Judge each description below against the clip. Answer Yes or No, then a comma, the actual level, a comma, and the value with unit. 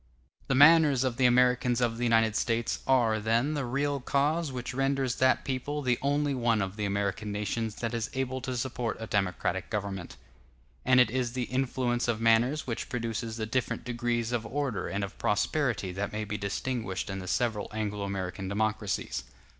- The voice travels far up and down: No, average, 3.5 semitones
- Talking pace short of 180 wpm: No, average, 185 wpm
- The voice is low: Yes, low, 120 Hz